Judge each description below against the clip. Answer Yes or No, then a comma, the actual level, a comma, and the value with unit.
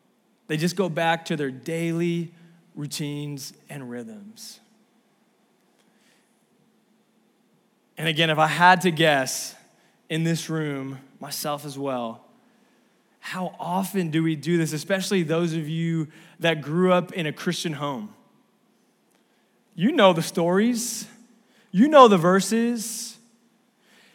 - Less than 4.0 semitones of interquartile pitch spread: No, wide, 5.6 semitones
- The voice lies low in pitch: No, medium, 180 Hz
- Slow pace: Yes, slow, 120 wpm